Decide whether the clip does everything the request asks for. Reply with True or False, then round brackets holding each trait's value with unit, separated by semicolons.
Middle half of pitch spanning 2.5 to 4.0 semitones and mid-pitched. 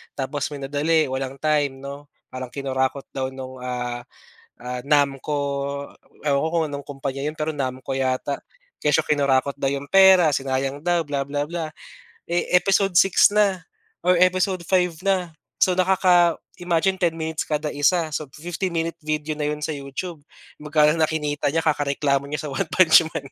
True (3.5 semitones; 150 Hz)